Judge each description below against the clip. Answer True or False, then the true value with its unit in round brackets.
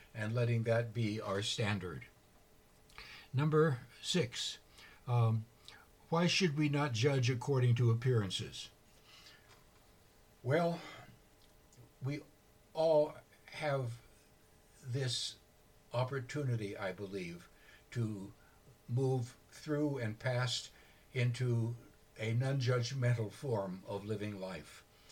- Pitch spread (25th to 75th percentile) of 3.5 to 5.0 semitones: True (4.6 semitones)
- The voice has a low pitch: True (120 Hz)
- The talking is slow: True (90 wpm)